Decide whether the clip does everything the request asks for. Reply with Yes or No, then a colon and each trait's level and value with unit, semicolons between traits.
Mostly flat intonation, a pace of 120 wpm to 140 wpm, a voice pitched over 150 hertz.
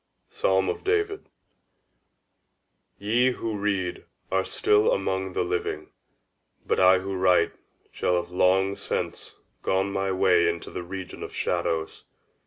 No: narrow, 1.5 semitones; slow, 135 wpm; very low, 95 Hz